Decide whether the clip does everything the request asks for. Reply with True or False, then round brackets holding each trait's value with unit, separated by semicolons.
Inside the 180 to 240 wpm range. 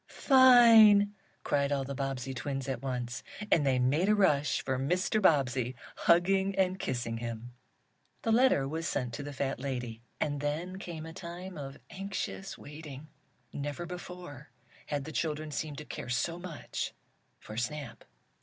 False (155 wpm)